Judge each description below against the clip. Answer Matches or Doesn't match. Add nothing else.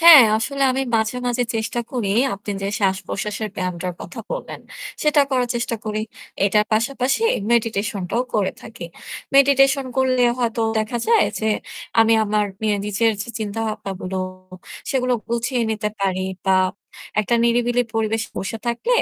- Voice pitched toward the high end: Matches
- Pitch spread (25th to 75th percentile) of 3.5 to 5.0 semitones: Doesn't match